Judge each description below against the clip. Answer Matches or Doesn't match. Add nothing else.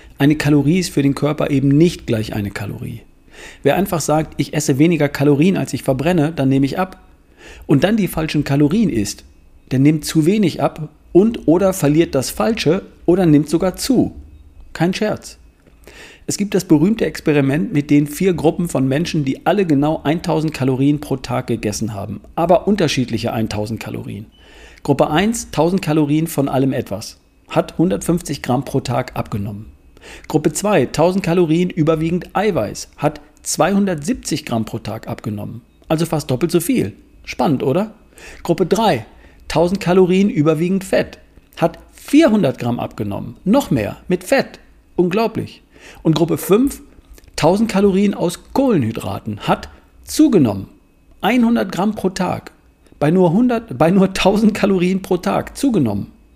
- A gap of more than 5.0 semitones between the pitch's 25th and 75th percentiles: Matches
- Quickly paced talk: Doesn't match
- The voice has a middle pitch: Matches